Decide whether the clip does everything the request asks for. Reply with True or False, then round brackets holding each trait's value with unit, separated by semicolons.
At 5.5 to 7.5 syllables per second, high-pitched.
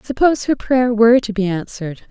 True (6.0 syllables/s; 230 Hz)